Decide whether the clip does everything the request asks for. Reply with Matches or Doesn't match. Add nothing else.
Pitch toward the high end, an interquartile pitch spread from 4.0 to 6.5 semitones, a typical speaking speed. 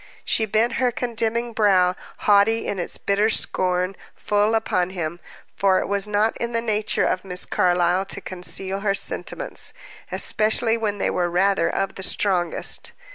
Doesn't match